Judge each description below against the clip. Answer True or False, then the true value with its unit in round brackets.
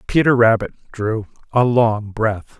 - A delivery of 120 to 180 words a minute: True (140 wpm)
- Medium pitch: False (115 Hz)